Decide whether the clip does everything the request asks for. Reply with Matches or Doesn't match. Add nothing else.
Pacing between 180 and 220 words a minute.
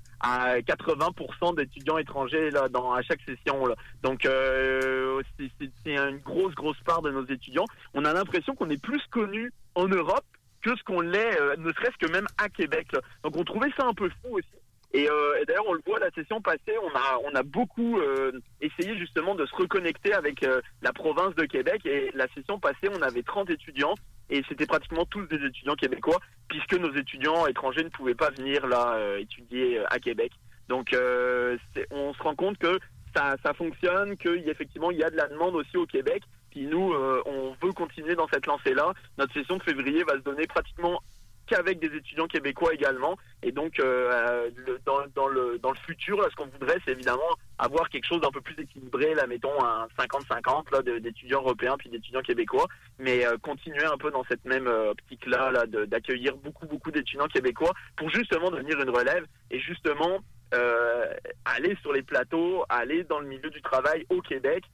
Matches